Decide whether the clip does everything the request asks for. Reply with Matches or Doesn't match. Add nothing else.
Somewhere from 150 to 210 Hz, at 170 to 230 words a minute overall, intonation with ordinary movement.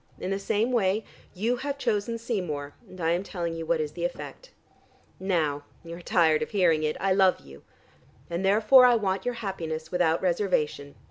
Matches